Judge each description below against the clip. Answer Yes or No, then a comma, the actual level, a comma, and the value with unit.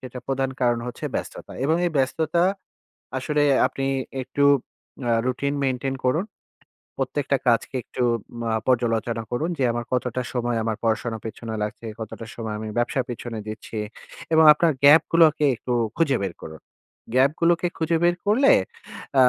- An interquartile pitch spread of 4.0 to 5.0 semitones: Yes, average, 4.3 semitones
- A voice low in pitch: Yes, low, 130 Hz